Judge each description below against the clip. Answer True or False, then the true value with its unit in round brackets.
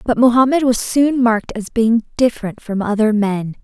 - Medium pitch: False (230 Hz)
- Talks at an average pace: True (180 wpm)